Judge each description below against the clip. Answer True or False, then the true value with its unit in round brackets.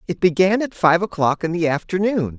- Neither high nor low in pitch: True (175 Hz)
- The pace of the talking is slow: False (200 wpm)